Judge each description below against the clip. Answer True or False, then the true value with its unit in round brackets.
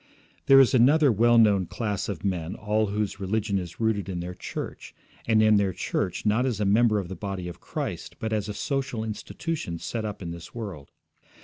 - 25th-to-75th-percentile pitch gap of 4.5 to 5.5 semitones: False (3.0 semitones)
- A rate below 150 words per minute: False (205 wpm)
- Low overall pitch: True (105 Hz)